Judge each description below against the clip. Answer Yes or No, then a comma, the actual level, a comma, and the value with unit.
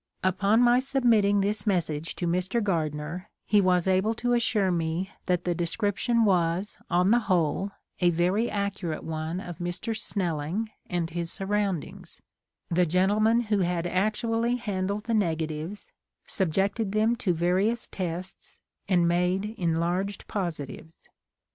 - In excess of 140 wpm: No, slow, 135 wpm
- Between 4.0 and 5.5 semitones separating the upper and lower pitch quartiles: No, average, 3.5 semitones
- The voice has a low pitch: No, medium, 185 Hz